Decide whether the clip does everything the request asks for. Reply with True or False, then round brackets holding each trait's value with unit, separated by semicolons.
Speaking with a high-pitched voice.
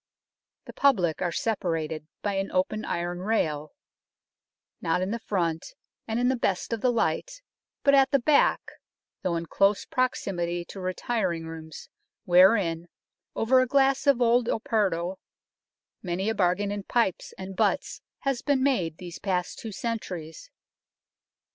True (195 Hz)